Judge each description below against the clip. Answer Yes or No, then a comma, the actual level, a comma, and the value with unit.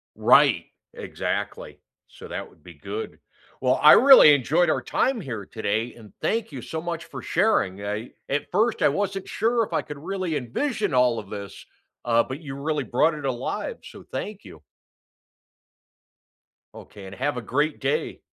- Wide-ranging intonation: Yes, wide, 8.7 semitones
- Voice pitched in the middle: Yes, medium, 145 Hz